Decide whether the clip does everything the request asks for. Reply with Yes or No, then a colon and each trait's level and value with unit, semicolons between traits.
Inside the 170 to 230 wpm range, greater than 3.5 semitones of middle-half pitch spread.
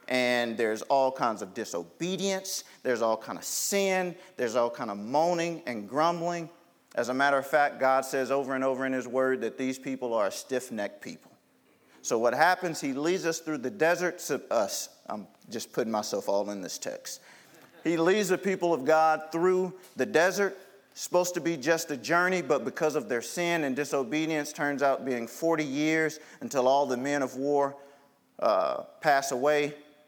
Yes: average, 185 wpm; average, 4.7 semitones